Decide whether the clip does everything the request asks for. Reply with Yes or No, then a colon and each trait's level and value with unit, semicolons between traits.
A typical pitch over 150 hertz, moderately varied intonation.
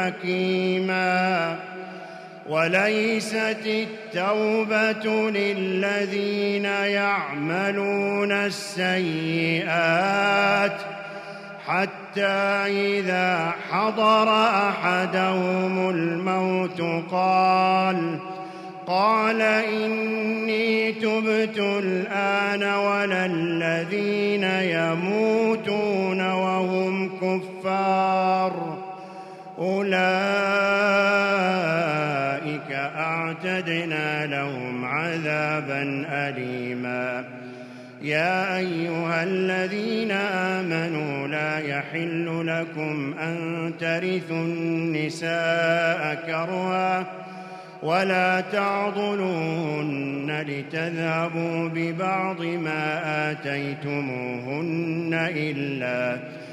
Yes: medium, 185 Hz; average, 3.4 semitones